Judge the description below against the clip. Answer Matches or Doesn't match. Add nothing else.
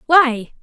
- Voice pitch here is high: Matches